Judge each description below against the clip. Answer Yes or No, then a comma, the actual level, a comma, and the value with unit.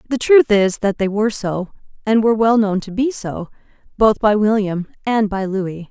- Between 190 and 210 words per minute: Yes, fast, 205 wpm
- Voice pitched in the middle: No, high, 210 Hz